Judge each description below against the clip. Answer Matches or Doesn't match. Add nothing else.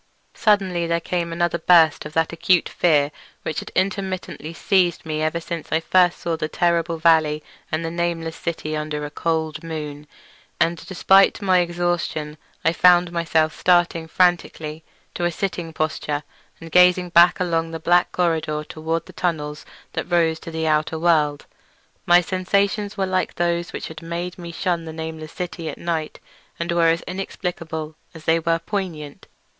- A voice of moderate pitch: Matches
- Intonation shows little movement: Matches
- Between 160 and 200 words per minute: Matches